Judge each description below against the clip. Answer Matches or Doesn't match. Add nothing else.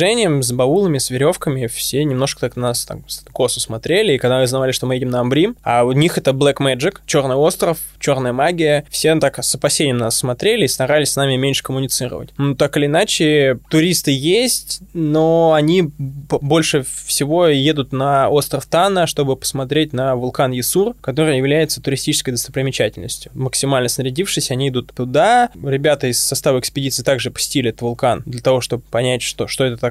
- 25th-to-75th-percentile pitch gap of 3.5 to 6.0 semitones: Doesn't match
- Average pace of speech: Doesn't match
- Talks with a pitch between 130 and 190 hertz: Matches